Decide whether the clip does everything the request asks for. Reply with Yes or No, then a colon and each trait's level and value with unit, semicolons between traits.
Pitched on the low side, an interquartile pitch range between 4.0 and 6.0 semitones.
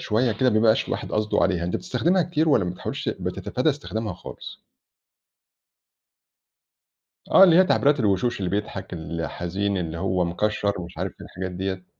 Yes: low, 100 Hz; wide, 5.6 semitones